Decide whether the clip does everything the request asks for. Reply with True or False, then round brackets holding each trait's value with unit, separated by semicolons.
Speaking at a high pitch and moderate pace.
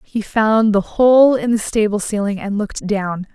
True (210 Hz; 195 wpm)